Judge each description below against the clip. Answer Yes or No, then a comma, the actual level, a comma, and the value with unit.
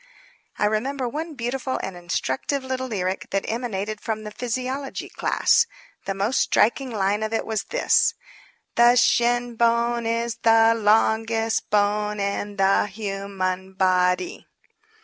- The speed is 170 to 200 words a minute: No, average, 145 wpm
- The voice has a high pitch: Yes, high, 220 Hz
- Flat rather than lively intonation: No, average, 3.4 semitones